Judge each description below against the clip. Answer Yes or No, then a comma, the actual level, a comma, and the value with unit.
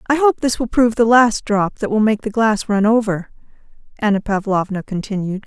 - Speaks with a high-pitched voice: Yes, high, 215 Hz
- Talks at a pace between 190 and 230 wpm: Yes, average, 200 wpm